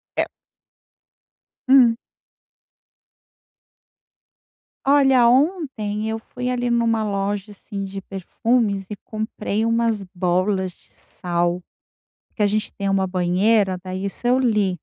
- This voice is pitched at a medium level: No, high, 210 Hz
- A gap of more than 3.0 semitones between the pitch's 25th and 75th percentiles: Yes, average, 3.5 semitones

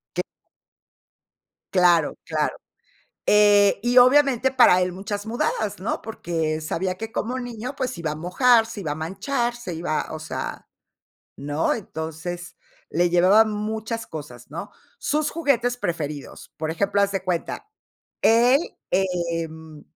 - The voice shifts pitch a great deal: Yes, wide, 6.1 semitones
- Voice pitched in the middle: No, high, 195 Hz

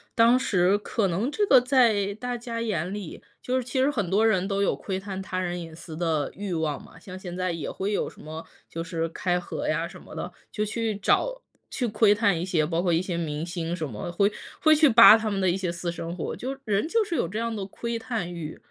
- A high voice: Yes, high, 195 Hz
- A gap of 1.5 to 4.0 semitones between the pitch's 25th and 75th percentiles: No, average, 4.9 semitones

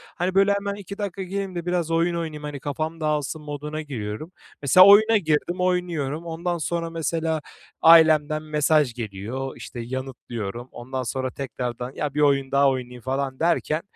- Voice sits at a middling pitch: Yes, medium, 155 Hz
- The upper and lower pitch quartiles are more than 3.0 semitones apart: Yes, average, 4.3 semitones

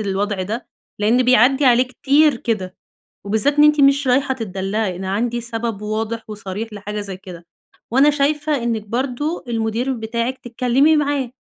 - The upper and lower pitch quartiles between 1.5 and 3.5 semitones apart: No, average, 4.2 semitones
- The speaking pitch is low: No, high, 235 Hz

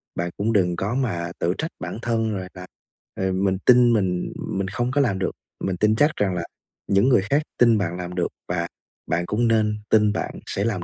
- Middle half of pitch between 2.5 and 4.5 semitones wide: Yes, average, 4.2 semitones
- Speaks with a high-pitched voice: No, low, 100 Hz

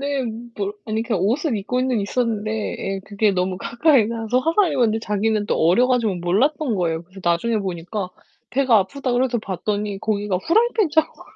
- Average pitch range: Yes, average, 4.4 semitones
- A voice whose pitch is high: Yes, high, 220 Hz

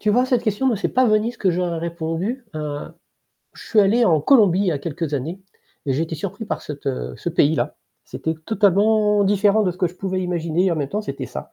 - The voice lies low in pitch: No, medium, 185 Hz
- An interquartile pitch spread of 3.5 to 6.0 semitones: Yes, average, 4.7 semitones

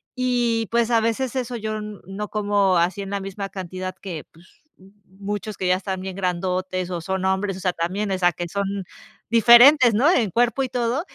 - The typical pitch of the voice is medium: No, high, 200 Hz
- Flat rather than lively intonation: No, average, 3.6 semitones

